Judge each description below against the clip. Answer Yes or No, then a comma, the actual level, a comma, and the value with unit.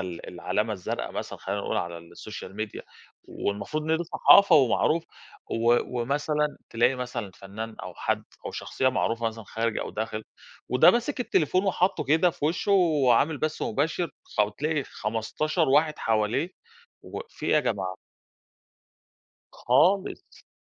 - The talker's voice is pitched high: No, low, 130 Hz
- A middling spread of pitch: No, wide, 6.5 semitones